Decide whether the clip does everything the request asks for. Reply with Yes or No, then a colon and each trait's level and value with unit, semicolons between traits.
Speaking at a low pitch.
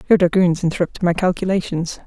No: medium, 175 Hz